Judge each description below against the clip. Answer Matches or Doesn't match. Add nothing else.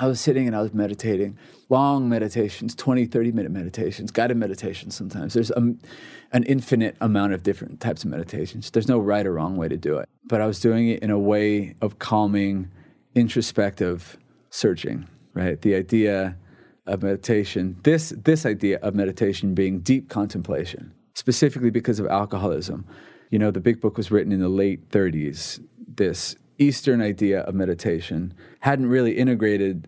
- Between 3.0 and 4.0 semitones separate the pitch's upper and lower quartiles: Matches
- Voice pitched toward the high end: Doesn't match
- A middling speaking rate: Matches